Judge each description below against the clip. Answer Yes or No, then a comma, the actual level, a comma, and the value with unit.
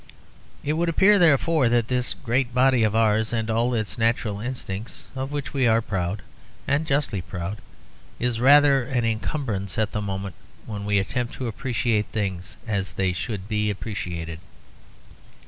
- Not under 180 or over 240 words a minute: No, average, 160 wpm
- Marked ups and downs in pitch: No, average, 4.2 semitones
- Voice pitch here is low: Yes, low, 115 Hz